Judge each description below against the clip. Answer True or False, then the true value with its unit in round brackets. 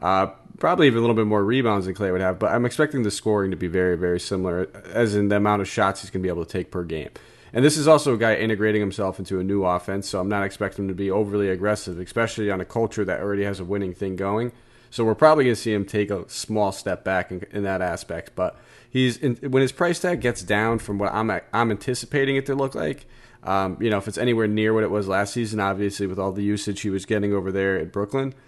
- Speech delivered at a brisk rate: True (270 wpm)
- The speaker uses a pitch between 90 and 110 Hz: True (105 Hz)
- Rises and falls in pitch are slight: False (3.1 semitones)